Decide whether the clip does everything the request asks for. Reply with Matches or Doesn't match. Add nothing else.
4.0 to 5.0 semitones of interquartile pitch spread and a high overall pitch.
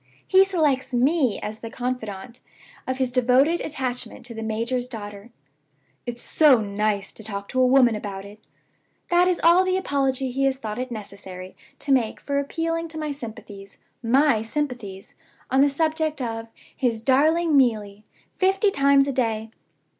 Matches